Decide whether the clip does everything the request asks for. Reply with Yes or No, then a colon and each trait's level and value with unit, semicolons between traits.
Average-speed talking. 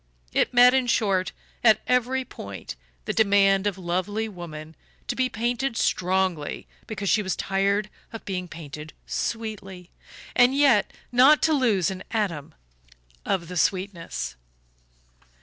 No: slow, 130 wpm